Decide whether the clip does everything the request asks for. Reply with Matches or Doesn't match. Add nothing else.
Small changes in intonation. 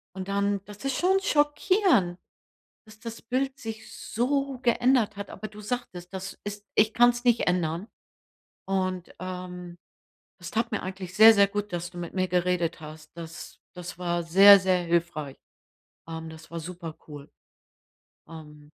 Doesn't match